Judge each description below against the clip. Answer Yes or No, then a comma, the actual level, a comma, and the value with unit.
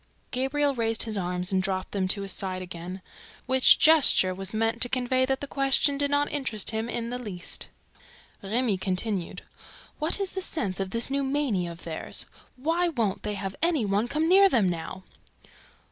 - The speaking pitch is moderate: No, high, 225 Hz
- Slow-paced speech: No, average, 185 wpm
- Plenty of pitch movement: Yes, wide, 6.4 semitones